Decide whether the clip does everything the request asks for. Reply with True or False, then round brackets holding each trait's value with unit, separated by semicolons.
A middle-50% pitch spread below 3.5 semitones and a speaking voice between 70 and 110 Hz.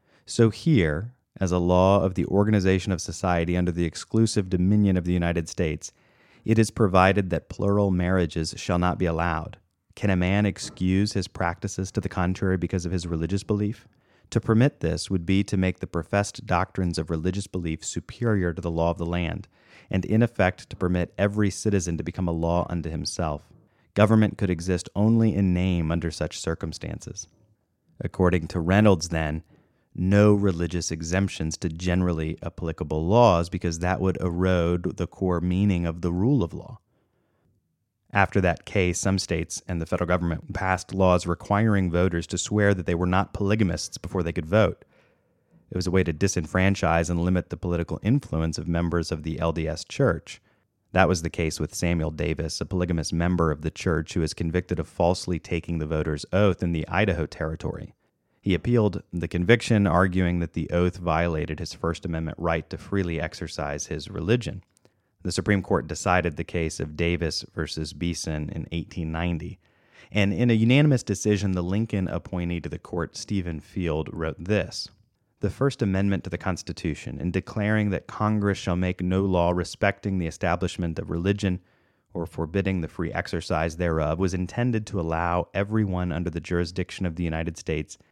True (2.9 semitones; 90 Hz)